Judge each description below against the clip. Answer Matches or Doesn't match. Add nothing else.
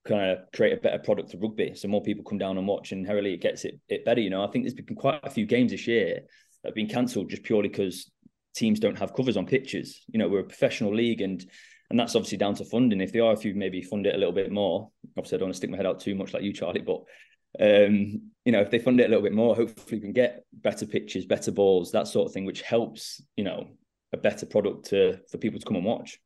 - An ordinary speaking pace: Doesn't match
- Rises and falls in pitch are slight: Doesn't match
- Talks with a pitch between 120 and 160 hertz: Doesn't match